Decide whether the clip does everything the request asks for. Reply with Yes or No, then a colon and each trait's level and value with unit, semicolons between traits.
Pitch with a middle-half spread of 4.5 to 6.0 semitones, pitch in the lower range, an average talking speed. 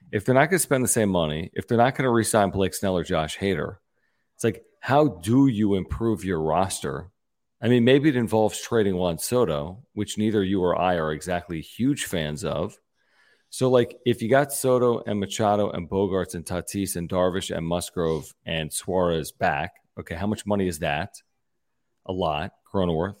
Yes: average, 4.9 semitones; low, 100 Hz; average, 195 wpm